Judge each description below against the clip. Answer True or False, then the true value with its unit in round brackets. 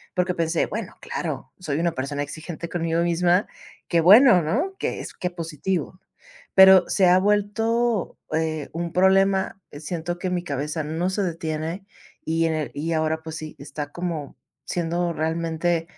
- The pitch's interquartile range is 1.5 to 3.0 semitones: True (2.6 semitones)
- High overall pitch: False (170 Hz)